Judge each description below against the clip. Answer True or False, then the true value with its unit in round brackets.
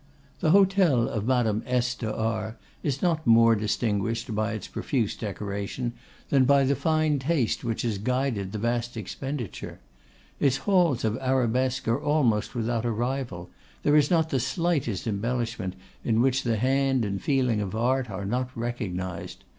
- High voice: False (120 Hz)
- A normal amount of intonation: True (3.6 semitones)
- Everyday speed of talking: True (160 wpm)